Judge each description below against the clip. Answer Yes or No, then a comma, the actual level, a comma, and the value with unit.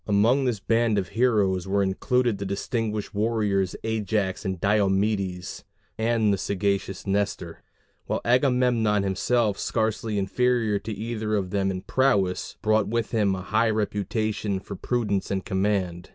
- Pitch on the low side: Yes, low, 105 Hz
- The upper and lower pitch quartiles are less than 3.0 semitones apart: Yes, narrow, 2.6 semitones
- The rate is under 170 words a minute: Yes, average, 140 wpm